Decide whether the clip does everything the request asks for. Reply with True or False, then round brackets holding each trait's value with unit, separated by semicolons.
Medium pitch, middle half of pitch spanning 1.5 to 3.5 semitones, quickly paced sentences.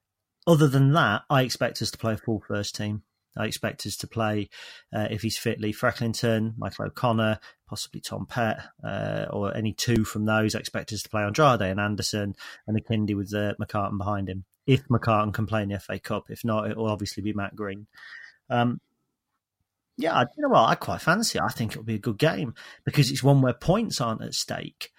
False (110 Hz; 3.1 semitones; 220 wpm)